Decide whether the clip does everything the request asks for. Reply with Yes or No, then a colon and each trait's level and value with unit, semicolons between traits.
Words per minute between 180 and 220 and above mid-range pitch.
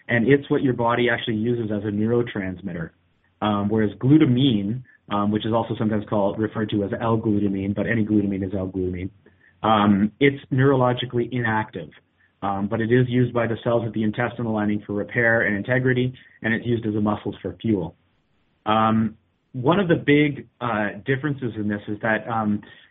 No: average, 190 wpm; low, 110 Hz